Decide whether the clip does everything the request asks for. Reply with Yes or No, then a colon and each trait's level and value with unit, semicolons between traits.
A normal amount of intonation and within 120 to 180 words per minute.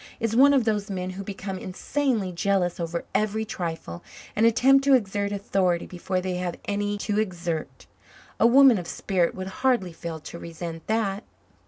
Yes: average, 3.6 semitones; average, 170 wpm